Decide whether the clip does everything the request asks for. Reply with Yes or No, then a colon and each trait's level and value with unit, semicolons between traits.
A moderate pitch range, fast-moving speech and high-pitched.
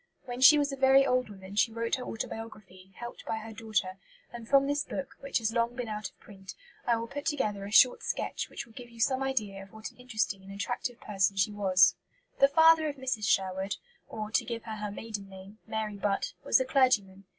Yes: average, 4.2 semitones; fast, 225 wpm; high, 225 Hz